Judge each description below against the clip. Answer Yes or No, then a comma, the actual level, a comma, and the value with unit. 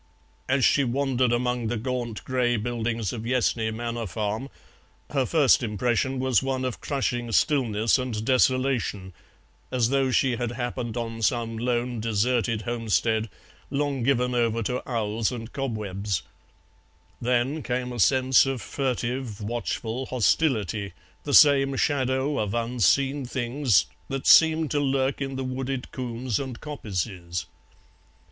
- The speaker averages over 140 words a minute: No, slow, 135 wpm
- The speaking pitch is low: Yes, low, 125 Hz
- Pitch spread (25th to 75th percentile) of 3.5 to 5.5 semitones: No, average, 2.7 semitones